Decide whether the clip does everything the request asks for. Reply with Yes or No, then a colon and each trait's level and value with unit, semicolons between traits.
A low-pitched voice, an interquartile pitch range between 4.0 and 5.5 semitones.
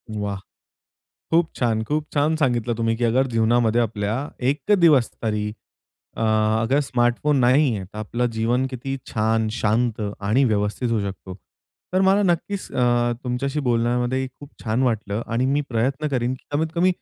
No: low, 120 Hz; average, 3.6 semitones